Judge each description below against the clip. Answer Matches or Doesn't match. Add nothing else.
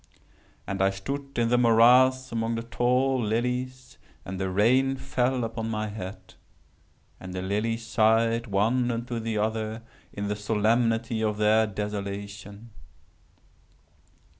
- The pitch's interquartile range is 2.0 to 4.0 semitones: Matches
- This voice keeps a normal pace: Doesn't match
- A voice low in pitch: Matches